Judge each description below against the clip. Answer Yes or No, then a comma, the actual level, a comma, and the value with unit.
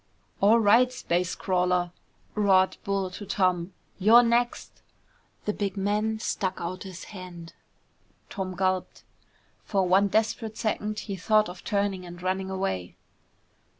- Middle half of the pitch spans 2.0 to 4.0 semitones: Yes, narrow, 2.6 semitones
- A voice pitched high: Yes, high, 195 Hz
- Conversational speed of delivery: No, slow, 130 wpm